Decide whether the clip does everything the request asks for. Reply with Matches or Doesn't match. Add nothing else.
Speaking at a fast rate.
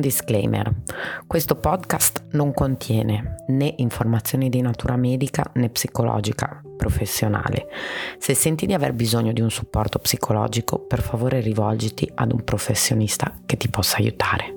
Doesn't match